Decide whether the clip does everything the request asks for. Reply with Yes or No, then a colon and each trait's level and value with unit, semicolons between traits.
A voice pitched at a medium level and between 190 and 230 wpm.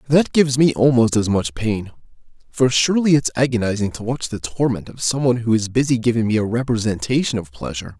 No: low, 120 Hz; average, 195 wpm